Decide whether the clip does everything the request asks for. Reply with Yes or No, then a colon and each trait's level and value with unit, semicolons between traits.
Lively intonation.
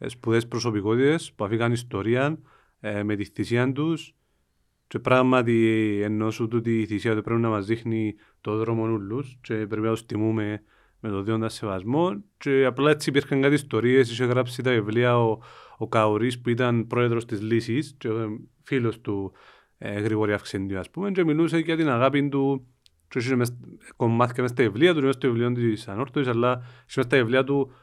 No: average, 3.4 semitones